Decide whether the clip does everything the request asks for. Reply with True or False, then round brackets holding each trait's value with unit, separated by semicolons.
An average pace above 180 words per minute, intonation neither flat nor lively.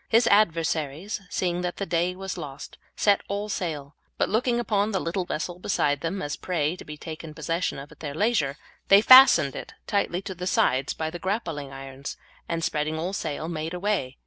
True (200 wpm; 4.6 semitones)